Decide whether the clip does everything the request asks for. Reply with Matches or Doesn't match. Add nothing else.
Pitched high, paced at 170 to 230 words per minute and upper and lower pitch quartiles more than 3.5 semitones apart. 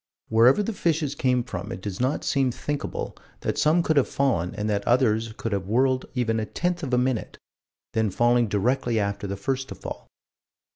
Doesn't match